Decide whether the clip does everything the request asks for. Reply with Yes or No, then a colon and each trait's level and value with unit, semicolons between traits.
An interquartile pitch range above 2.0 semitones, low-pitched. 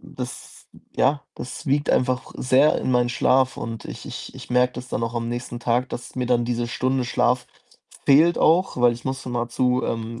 No: narrow, 1.5 semitones; low, 125 Hz